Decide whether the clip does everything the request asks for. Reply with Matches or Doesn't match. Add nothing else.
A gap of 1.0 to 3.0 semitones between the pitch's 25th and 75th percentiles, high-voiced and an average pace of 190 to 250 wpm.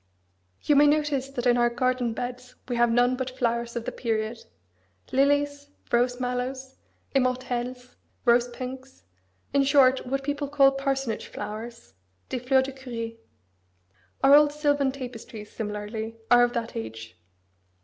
Doesn't match